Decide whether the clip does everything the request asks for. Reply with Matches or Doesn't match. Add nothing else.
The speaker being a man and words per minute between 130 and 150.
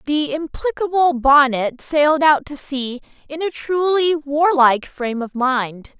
Doesn't match